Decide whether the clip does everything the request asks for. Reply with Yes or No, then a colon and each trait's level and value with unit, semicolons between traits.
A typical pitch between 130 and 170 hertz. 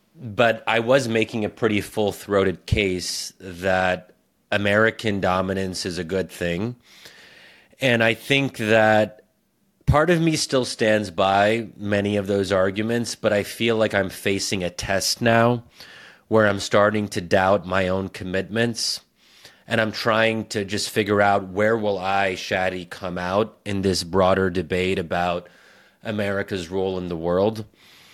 No: low, 100 Hz